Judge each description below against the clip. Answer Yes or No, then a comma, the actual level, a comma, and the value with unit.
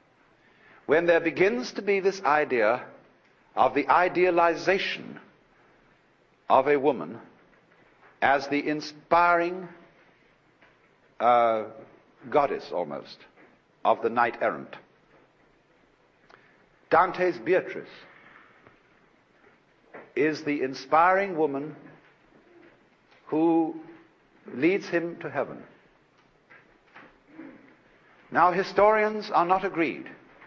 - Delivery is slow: Yes, slow, 75 wpm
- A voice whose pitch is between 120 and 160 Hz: No, medium, 170 Hz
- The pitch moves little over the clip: No, average, 3.6 semitones